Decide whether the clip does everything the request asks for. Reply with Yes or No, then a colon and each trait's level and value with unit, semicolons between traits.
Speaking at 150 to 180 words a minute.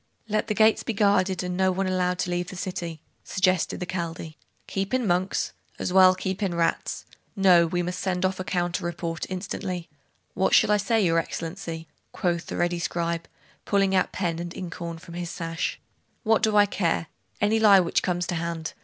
No: average, 195 wpm